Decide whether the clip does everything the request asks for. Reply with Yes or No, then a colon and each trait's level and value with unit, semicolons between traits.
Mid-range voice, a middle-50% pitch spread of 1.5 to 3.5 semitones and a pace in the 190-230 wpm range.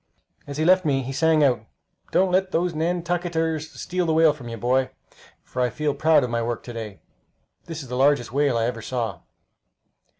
No: medium, 145 Hz; average, 4.9 semitones; average, 200 wpm